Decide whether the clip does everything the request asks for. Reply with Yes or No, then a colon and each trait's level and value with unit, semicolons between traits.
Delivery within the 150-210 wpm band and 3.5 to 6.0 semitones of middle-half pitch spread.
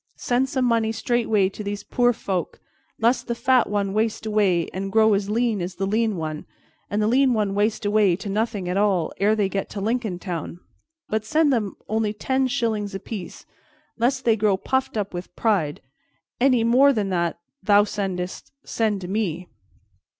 No: average, 185 wpm; average, 3.0 semitones